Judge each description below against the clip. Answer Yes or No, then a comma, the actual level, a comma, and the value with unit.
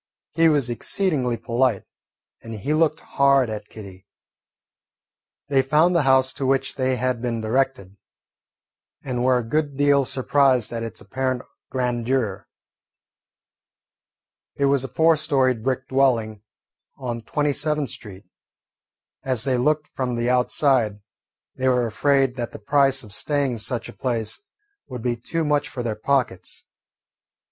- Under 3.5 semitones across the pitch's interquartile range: Yes, average, 3.0 semitones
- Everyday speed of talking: Yes, average, 145 wpm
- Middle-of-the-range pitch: No, low, 130 Hz